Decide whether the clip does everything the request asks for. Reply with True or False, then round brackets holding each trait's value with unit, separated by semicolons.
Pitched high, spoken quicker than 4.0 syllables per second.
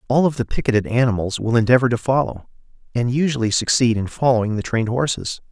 False (120 Hz; 6.5 syllables/s)